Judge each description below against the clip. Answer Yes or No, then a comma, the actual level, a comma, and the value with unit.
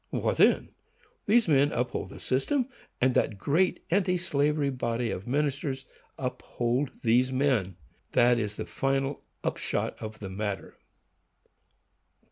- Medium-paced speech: No, slow, 125 wpm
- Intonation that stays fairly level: No, average, 3.6 semitones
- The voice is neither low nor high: No, low, 130 Hz